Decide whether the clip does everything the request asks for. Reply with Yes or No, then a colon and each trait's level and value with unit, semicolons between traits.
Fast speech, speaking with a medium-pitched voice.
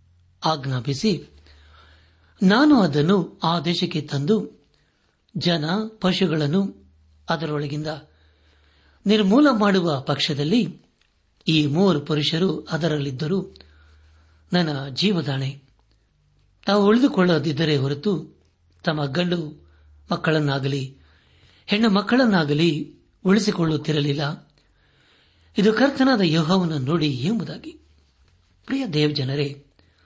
No: average, 70 wpm; medium, 150 Hz